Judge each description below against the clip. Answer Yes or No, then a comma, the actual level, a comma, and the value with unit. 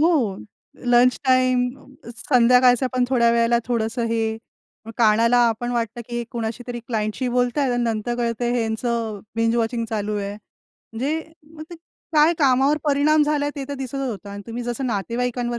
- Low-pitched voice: No, high, 240 Hz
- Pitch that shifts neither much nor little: No, narrow, 2.2 semitones